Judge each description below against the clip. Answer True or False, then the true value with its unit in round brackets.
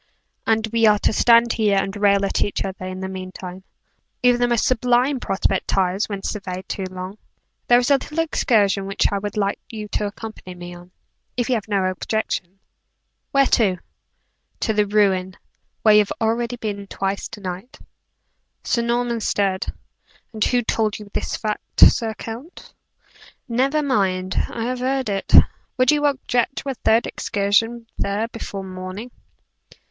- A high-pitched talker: True (210 Hz)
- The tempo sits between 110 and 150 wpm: False (175 wpm)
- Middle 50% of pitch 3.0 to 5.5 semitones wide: True (3.6 semitones)